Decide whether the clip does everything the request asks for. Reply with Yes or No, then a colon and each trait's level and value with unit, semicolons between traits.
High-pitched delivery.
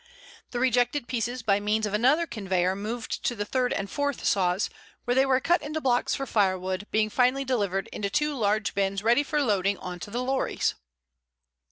Yes: high, 225 Hz